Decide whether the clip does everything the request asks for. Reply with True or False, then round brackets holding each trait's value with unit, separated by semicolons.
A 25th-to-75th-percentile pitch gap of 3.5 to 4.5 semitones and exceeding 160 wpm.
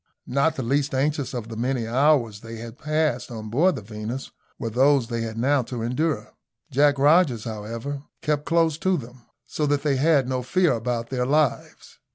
True (4.0 semitones; 195 wpm)